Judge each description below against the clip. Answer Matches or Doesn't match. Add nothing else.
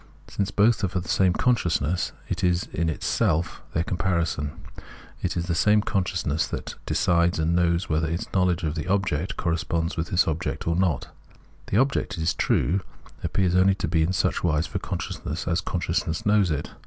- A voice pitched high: Doesn't match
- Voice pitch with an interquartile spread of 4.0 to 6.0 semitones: Doesn't match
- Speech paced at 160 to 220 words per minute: Matches